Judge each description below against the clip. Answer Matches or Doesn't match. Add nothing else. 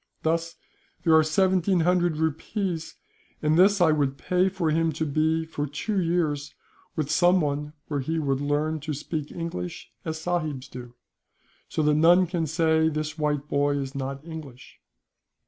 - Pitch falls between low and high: Matches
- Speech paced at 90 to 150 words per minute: Doesn't match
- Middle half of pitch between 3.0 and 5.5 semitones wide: Doesn't match